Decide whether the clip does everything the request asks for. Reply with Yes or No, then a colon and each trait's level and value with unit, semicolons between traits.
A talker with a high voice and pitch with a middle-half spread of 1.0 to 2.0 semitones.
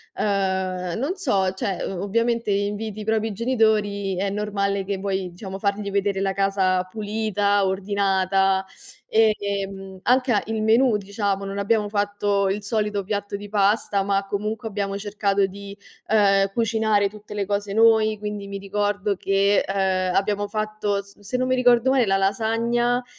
Yes: high, 205 Hz; narrow, 1.6 semitones